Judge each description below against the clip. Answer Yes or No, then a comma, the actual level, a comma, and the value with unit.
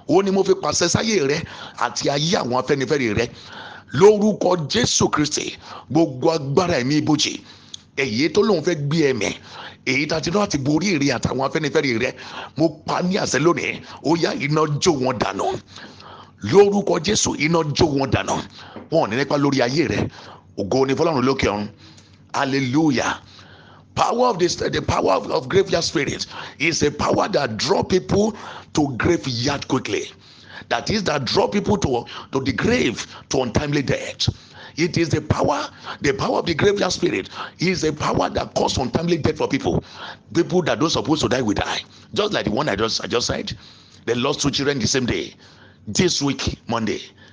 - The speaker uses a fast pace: No, average, 170 wpm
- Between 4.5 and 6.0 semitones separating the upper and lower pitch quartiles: Yes, average, 5.2 semitones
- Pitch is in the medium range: Yes, medium, 155 Hz